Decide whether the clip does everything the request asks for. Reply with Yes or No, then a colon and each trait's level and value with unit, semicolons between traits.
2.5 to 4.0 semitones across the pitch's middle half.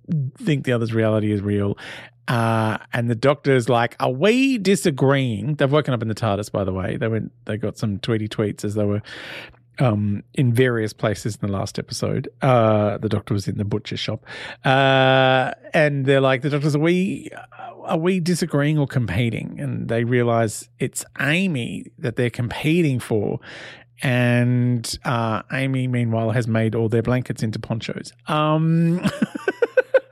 No: average, 4.9 semitones